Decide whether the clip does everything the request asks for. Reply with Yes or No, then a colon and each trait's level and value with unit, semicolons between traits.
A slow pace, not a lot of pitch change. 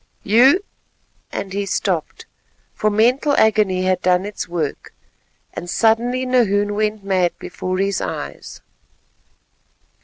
No: slow, 115 wpm; average, 3.3 semitones